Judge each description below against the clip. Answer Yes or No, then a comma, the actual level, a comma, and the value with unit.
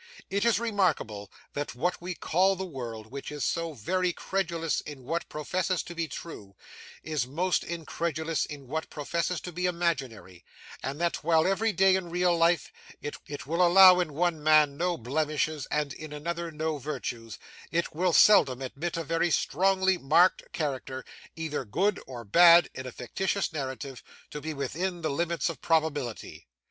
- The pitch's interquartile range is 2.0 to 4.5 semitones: Yes, average, 3.9 semitones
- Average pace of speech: Yes, average, 165 wpm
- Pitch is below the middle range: No, medium, 160 Hz